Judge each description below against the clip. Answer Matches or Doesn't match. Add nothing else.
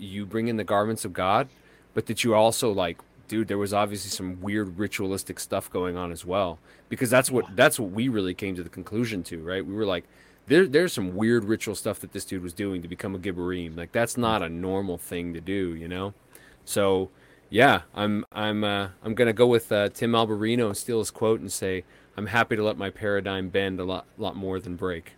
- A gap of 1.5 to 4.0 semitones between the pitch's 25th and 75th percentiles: Matches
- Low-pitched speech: Matches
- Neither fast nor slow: Doesn't match